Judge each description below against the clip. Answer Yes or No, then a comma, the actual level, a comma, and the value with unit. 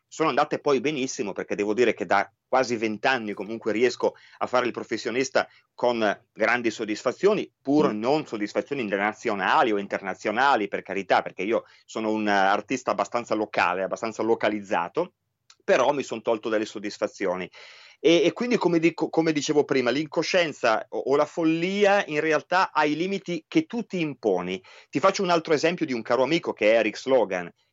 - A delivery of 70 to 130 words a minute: No, fast, 170 wpm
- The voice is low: No, medium, 145 Hz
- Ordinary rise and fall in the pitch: No, wide, 7.1 semitones